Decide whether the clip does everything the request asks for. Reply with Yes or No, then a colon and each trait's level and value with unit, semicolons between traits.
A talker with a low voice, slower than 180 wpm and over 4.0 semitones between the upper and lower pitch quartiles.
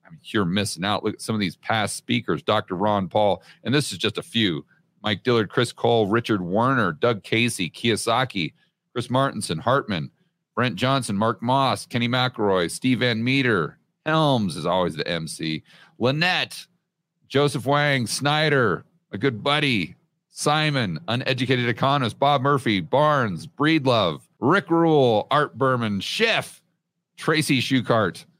Yes: low, 130 Hz; average, 145 wpm; average, 5.0 semitones